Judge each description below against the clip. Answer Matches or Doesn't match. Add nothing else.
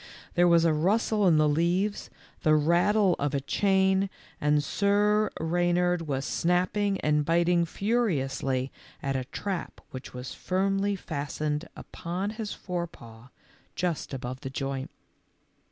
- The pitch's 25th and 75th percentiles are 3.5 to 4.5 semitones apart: Doesn't match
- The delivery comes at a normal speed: Doesn't match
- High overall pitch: Doesn't match